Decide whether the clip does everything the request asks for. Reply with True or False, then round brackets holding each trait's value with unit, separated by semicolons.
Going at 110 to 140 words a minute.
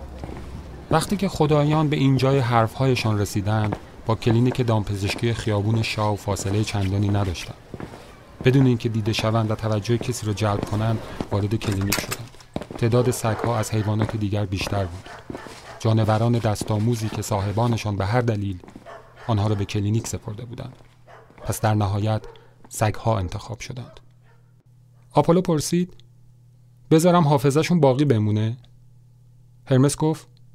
True (125 wpm)